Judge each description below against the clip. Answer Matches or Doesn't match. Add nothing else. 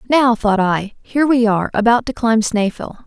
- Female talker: Matches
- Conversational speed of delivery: Matches